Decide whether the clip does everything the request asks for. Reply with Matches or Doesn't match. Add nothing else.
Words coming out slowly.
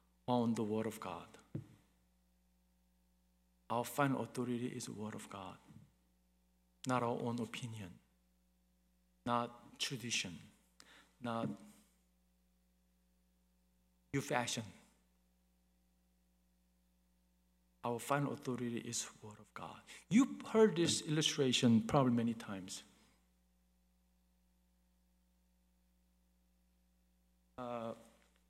Matches